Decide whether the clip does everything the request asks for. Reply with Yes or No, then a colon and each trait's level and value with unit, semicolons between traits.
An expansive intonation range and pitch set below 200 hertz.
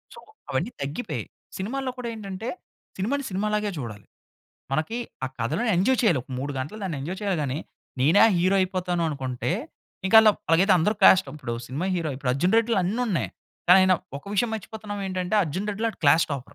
Yes: wide, 5.9 semitones; medium, 185 Hz